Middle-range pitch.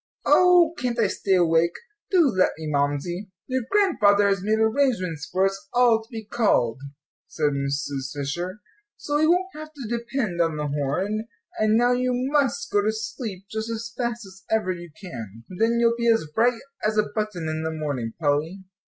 No: high, 210 Hz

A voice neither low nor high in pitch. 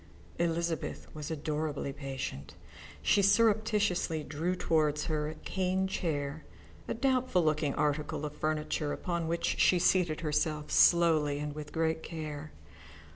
Yes: medium, 155 Hz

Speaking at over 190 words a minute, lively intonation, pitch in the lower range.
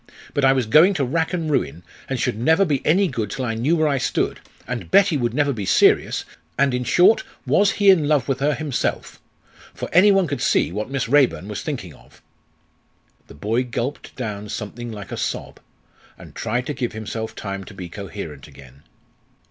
Yes: average, 200 wpm; wide, 6.2 semitones; low, 125 Hz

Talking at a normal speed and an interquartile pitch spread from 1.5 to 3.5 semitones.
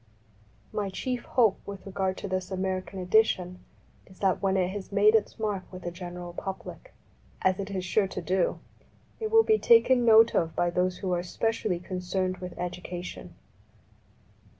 Yes: average, 175 wpm; narrow, 2.5 semitones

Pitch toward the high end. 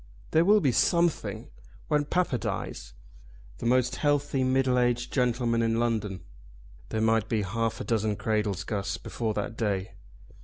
No: low, 115 Hz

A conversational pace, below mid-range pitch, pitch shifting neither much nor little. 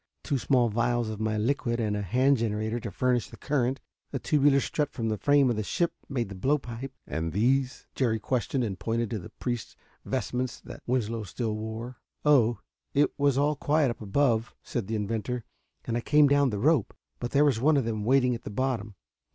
No: fast, 210 wpm; low, 120 Hz; average, 3.6 semitones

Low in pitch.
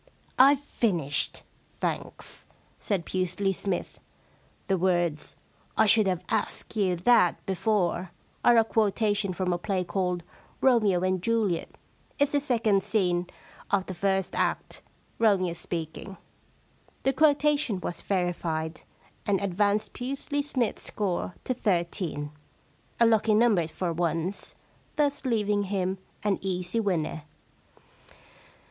No: high, 195 Hz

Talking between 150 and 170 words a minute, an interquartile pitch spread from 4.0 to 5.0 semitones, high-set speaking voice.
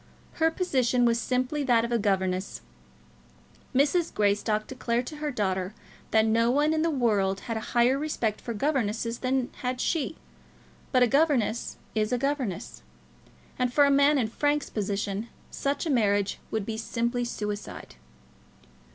Yes: average, 160 wpm; average, 4.5 semitones; high, 240 Hz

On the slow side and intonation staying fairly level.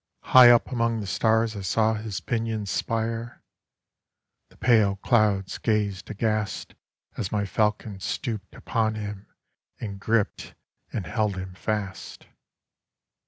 Yes: slow, 115 wpm; narrow, 2.2 semitones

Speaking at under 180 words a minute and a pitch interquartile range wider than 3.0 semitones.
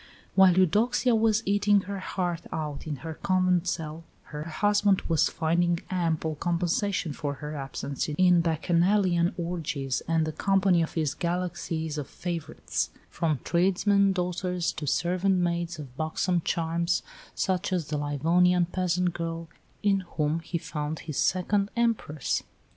No: average, 140 wpm; average, 2.7 semitones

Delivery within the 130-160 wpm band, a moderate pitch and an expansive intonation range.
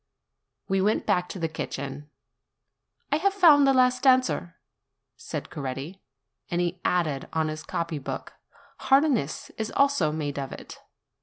Yes: average, 145 wpm; medium, 175 Hz; wide, 8.9 semitones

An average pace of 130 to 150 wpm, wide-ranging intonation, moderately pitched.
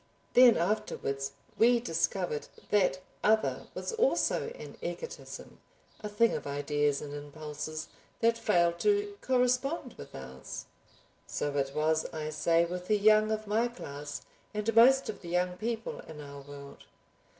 Yes: average, 145 wpm; wide, 7.6 semitones; medium, 180 Hz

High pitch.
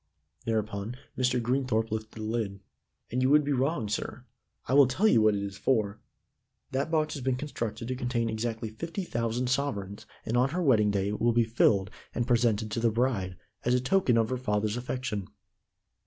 No: low, 115 Hz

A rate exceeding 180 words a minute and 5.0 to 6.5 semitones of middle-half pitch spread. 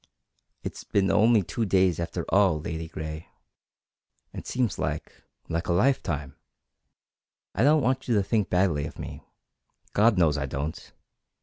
No: average, 140 wpm; wide, 5.6 semitones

